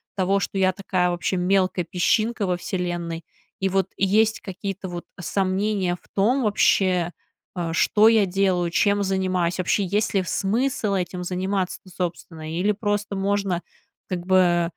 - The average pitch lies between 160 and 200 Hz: Yes, high, 190 Hz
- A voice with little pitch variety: Yes, narrow, 2.1 semitones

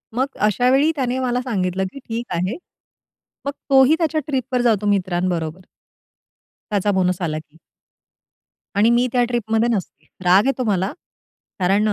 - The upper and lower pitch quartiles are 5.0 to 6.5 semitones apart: Yes, wide, 5.4 semitones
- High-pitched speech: Yes, high, 220 Hz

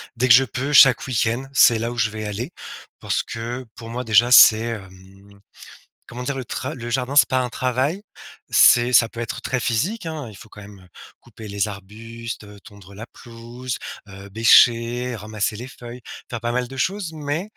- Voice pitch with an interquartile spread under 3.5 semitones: Yes, average, 2.8 semitones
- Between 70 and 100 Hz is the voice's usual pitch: No, low, 120 Hz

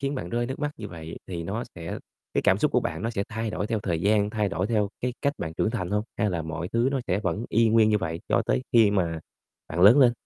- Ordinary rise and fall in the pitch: Yes, average, 5.0 semitones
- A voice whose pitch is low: Yes, low, 105 Hz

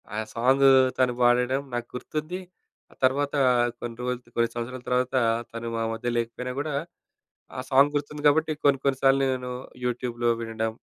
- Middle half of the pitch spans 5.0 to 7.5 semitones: No, narrow, 2.5 semitones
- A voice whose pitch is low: Yes, low, 125 Hz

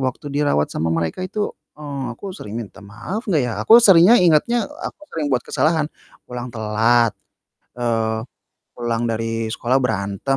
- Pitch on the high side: No, low, 125 Hz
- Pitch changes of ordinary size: No, wide, 6.1 semitones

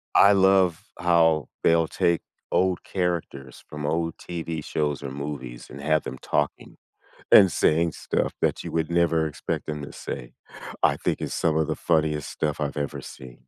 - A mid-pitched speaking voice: No, very low, 80 Hz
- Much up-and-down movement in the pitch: No, narrow, 2.6 semitones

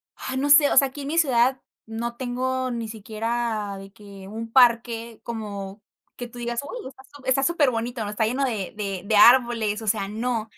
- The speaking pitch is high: Yes, high, 235 Hz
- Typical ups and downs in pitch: Yes, average, 3.3 semitones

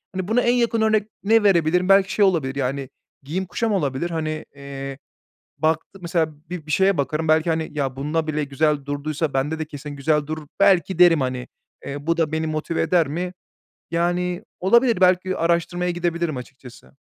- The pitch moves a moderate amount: Yes, average, 3.7 semitones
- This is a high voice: No, medium, 160 Hz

